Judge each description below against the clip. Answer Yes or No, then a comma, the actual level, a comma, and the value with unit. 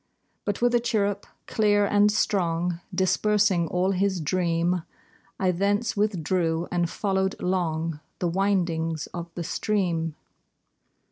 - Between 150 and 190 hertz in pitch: Yes, medium, 185 Hz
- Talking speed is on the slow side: Yes, slow, 120 wpm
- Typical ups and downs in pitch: Yes, average, 3.2 semitones